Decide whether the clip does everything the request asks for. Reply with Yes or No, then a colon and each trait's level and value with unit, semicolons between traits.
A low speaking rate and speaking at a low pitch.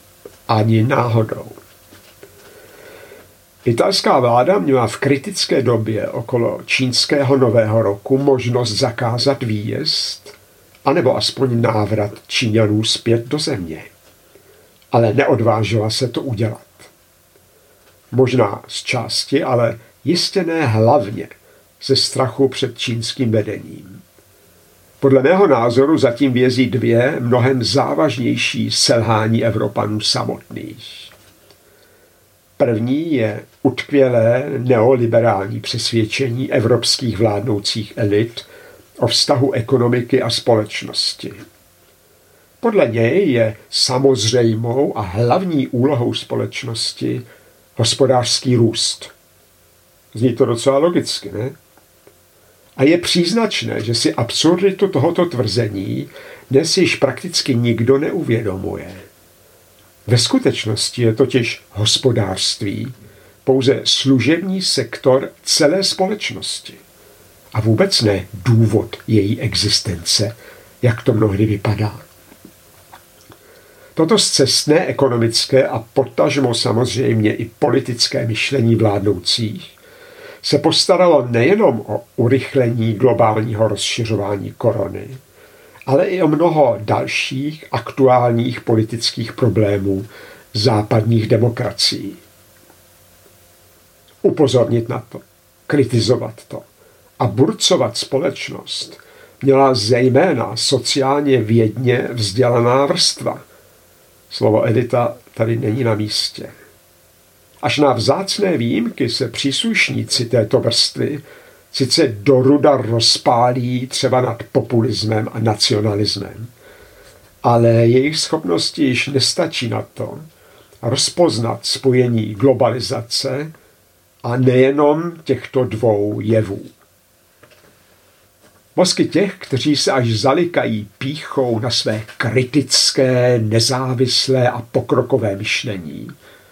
Yes: slow, 90 wpm; low, 120 Hz